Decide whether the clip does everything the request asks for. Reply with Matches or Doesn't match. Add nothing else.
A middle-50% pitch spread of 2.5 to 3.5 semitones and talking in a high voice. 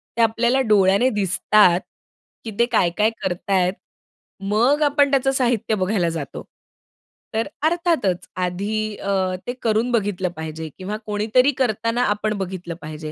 Doesn't match